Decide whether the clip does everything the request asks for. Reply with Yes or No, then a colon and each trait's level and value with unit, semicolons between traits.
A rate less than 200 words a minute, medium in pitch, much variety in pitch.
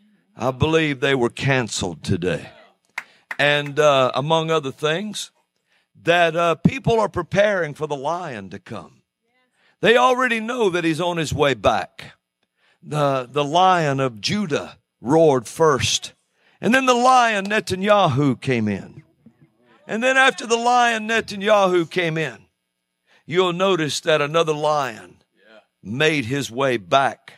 Yes: slow, 135 wpm; medium, 155 Hz; wide, 6.8 semitones